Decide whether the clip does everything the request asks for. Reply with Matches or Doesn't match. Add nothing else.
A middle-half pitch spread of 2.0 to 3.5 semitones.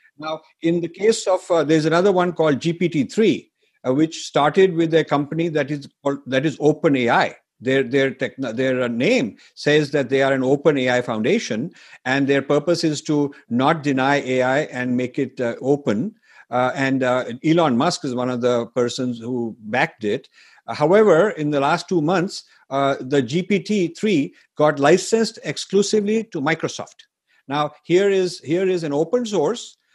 Doesn't match